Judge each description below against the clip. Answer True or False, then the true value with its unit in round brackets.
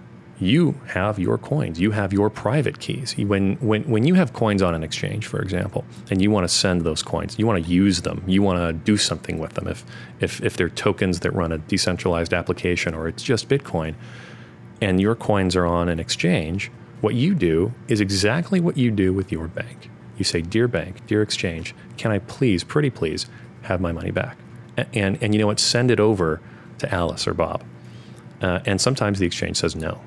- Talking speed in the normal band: False (210 wpm)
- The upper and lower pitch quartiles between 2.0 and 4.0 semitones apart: False (4.7 semitones)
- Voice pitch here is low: True (100 Hz)